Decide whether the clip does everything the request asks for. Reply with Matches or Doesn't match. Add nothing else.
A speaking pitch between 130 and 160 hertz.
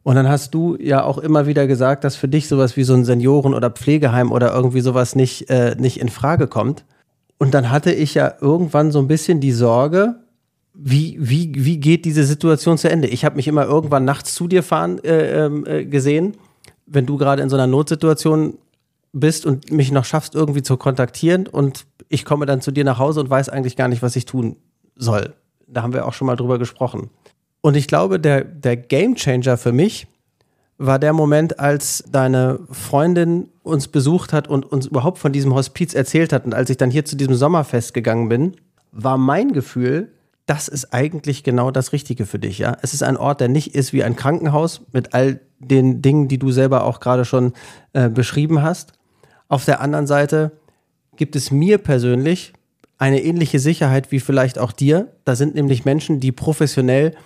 Matches